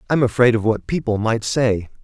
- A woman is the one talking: No, male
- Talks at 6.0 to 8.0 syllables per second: No, 5.2 syllables/s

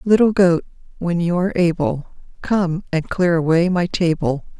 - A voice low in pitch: No, medium, 175 Hz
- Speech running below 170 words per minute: Yes, average, 155 wpm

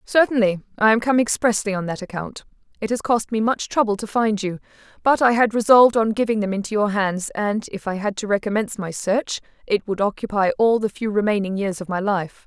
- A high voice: Yes, high, 210 Hz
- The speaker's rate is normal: No, fast, 220 wpm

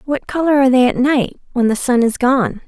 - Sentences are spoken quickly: Yes, fast, 245 wpm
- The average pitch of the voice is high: Yes, very high, 260 Hz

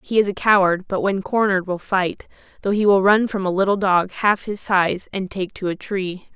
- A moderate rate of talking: No, fast, 235 wpm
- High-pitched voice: Yes, high, 195 Hz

